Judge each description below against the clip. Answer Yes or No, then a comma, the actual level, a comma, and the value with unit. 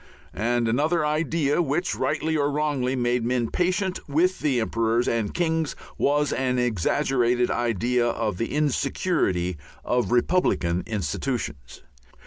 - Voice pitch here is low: Yes, low, 125 Hz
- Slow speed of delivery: Yes, slow, 120 wpm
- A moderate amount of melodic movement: Yes, average, 4.6 semitones